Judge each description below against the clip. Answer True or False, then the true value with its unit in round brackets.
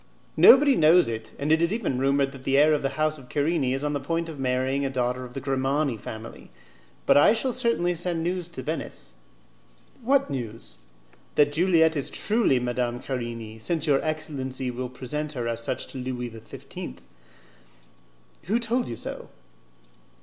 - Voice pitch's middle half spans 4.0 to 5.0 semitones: True (4.6 semitones)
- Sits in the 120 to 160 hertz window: True (140 Hz)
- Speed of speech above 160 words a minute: True (180 wpm)